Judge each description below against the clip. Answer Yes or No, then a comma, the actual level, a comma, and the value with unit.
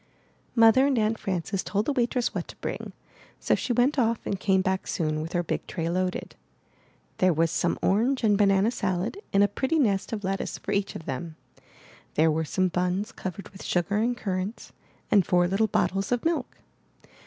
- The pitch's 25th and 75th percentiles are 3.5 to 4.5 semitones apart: Yes, average, 3.9 semitones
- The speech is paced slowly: No, average, 190 wpm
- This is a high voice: Yes, high, 195 Hz